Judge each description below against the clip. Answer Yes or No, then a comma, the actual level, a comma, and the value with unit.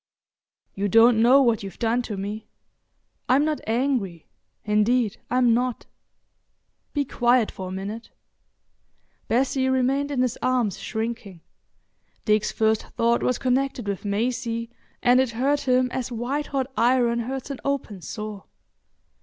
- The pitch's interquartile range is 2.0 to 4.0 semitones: Yes, average, 2.9 semitones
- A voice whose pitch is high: Yes, high, 240 Hz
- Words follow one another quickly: No, slow, 135 wpm